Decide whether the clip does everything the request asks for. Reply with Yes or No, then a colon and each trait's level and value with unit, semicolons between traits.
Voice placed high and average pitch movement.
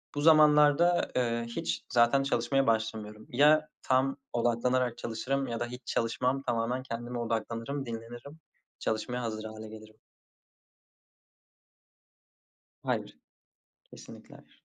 No: low, 120 Hz; average, 3.1 semitones